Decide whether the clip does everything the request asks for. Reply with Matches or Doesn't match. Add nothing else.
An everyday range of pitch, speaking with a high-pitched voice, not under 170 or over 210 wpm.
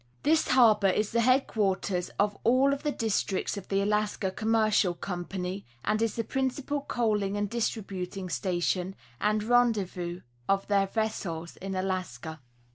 Doesn't match